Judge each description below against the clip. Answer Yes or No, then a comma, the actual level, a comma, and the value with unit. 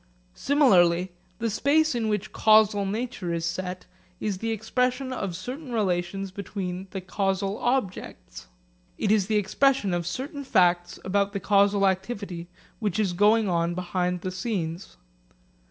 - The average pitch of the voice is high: Yes, high, 195 Hz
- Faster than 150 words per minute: No, average, 140 wpm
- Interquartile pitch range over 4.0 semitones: No, average, 3.6 semitones